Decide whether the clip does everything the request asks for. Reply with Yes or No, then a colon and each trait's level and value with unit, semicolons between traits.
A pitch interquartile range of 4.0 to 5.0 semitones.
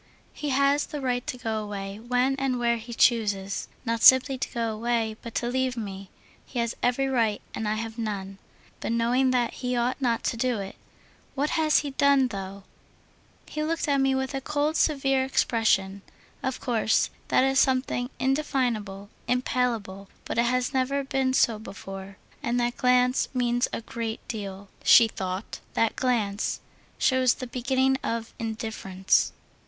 No: average, 3.2 semitones